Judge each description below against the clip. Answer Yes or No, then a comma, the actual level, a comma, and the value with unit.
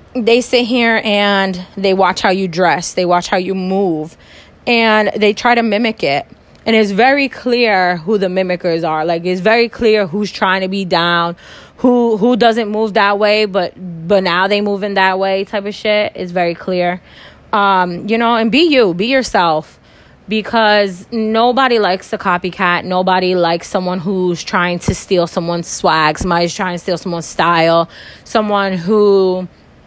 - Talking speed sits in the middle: Yes, average, 175 wpm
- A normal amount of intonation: Yes, average, 3.3 semitones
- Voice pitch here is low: No, high, 195 Hz